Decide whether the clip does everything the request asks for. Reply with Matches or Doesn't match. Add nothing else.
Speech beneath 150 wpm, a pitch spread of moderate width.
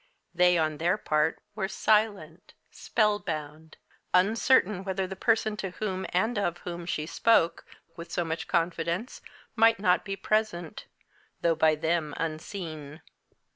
Matches